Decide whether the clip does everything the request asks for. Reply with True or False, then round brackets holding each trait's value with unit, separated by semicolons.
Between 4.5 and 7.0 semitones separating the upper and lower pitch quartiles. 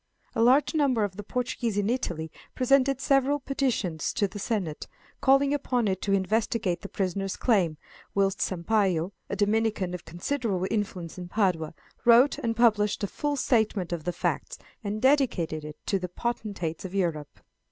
True (5.2 semitones)